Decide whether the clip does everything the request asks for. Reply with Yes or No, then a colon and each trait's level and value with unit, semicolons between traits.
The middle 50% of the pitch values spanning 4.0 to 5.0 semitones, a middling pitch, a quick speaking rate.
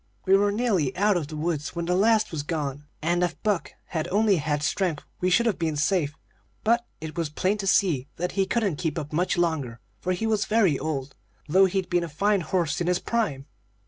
Yes: average, 4.5 semitones; medium, 175 Hz; fast, 220 wpm